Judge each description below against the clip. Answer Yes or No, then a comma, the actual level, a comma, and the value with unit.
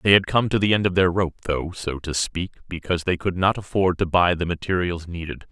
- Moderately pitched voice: No, very low, 90 Hz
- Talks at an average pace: No, fast, 250 wpm